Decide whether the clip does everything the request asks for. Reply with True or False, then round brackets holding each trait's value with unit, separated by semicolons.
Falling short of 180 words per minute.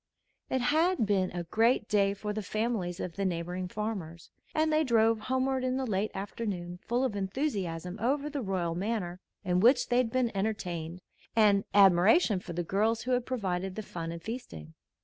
False (185 wpm)